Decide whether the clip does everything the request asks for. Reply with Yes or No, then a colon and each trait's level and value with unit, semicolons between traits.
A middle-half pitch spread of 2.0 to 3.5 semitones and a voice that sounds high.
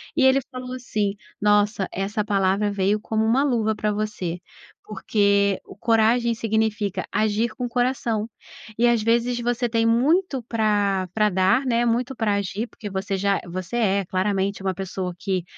Yes: average, 3.0 semitones; high, 215 Hz